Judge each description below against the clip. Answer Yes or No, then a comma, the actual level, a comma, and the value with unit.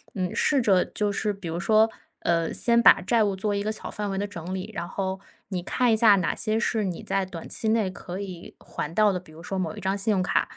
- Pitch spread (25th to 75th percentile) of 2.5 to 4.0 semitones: Yes, average, 2.9 semitones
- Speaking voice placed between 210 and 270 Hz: No, high, 195 Hz